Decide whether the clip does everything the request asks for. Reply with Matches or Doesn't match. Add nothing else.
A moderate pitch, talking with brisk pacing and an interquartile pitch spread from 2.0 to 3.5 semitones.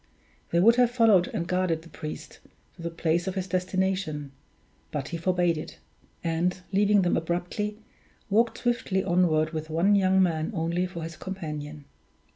Doesn't match